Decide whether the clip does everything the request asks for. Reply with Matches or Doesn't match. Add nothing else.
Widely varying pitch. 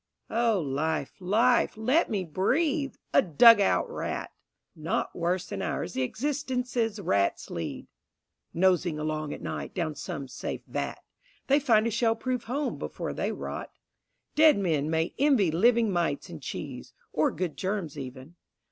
Matches